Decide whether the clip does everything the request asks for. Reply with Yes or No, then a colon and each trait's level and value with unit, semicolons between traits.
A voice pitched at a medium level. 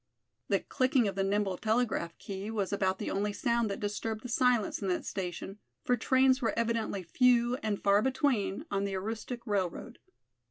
No: high, 210 Hz